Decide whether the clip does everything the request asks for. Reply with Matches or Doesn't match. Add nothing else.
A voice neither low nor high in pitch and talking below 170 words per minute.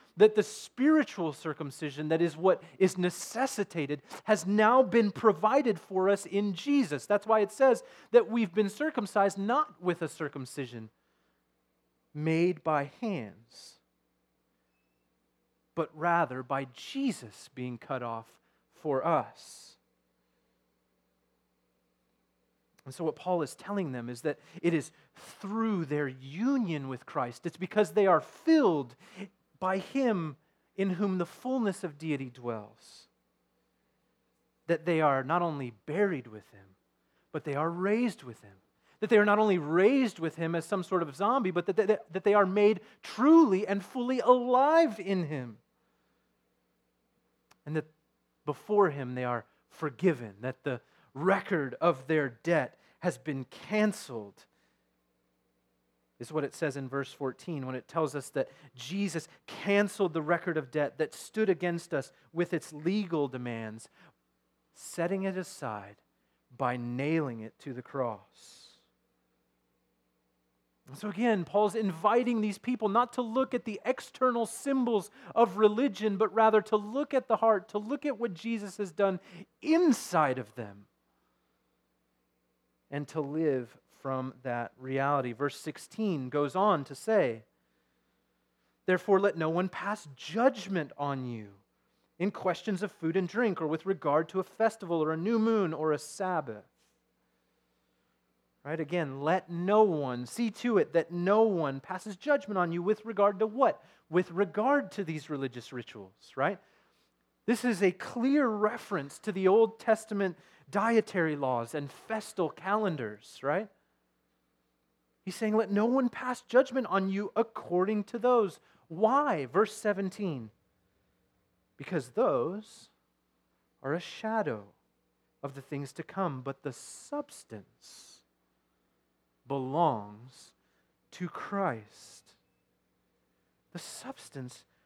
Matches